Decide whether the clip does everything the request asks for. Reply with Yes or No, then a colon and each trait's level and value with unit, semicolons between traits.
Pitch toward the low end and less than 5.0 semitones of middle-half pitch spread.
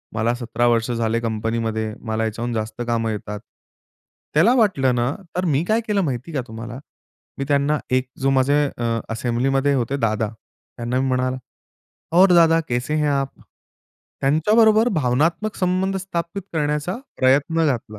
No: low, 130 Hz; wide, 5.7 semitones